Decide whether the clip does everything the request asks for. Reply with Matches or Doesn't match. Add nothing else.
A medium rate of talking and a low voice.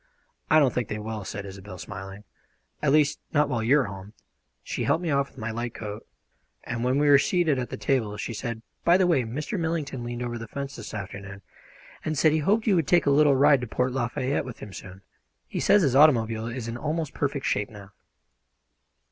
Doesn't match